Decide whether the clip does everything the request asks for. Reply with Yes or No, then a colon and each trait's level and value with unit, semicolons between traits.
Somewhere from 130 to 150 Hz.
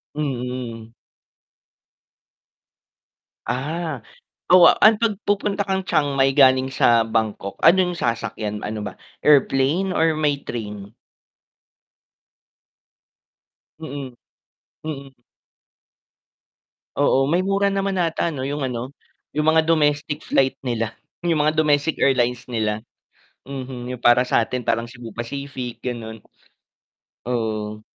Yes: low, 135 Hz